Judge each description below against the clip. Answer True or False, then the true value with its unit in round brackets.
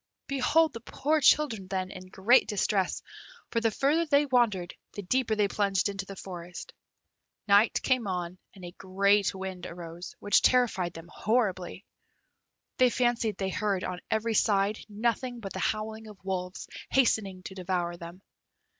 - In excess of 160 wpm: False (155 wpm)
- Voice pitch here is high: True (200 Hz)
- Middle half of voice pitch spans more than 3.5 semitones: True (4.0 semitones)